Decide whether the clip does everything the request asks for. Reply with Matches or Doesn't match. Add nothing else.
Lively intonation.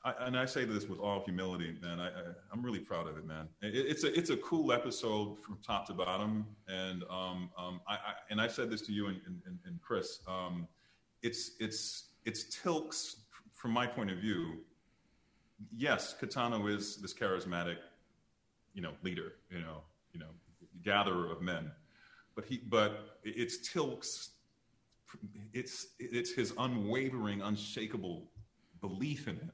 Doesn't match